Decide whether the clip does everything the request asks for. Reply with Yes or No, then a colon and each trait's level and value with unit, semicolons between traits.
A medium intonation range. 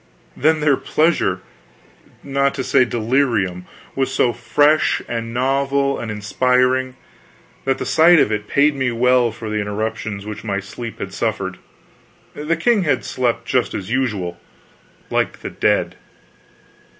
Yes: average, 4.1 semitones